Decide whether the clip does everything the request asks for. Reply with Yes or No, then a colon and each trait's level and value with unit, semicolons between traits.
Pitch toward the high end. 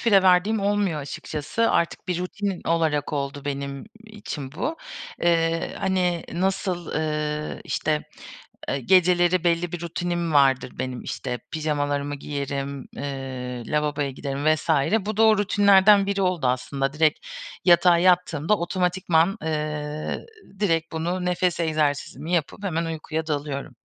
No: medium, 160 Hz